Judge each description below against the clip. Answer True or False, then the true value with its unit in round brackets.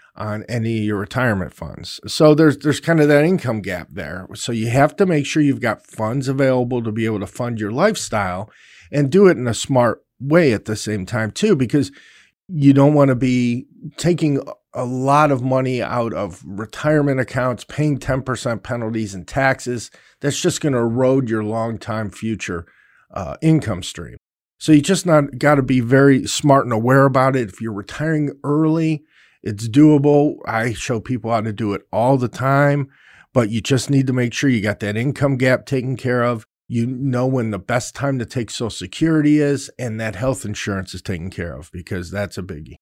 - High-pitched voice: False (125 Hz)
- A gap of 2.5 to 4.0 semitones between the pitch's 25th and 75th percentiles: False (4.4 semitones)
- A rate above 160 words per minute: True (200 wpm)